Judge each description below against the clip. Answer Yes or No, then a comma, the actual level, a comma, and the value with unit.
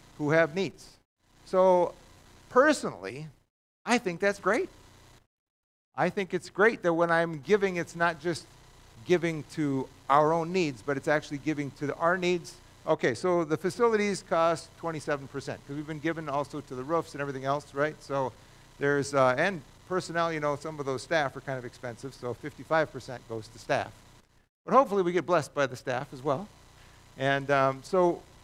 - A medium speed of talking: Yes, average, 175 wpm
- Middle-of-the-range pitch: Yes, medium, 150 Hz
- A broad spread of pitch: No, average, 4.3 semitones